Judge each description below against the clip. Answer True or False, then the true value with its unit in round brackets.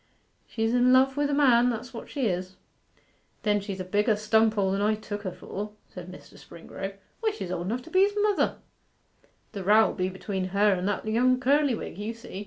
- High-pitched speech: True (215 Hz)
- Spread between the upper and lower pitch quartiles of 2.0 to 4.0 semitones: False (4.4 semitones)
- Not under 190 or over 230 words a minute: True (200 wpm)